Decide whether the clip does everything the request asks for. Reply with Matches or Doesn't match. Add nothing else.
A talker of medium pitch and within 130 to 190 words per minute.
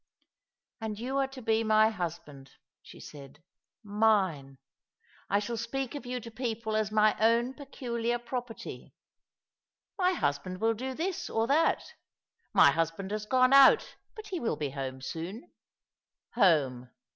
Doesn't match